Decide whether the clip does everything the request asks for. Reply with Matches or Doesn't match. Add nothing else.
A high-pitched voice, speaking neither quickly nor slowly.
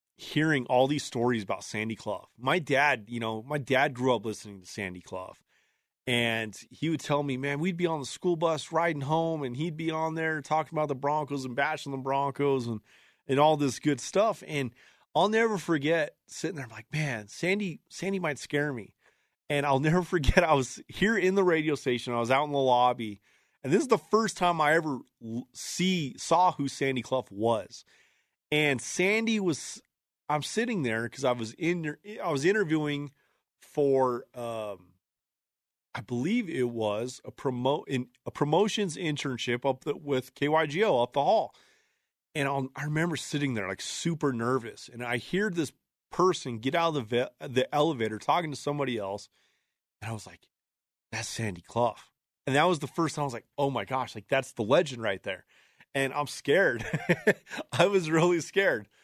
Doesn't match